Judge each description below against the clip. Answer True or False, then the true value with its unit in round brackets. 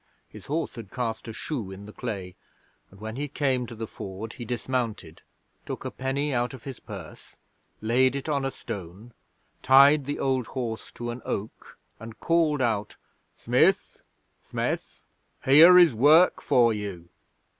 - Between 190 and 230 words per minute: False (160 wpm)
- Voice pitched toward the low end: True (120 Hz)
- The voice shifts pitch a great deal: False (4.0 semitones)